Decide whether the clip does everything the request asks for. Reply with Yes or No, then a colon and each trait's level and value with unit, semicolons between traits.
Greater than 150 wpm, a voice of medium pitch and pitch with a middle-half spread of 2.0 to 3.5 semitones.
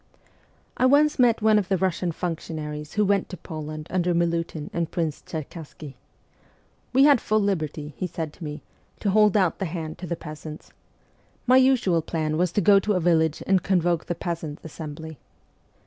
No: average, 185 wpm; medium, 170 Hz; average, 3.9 semitones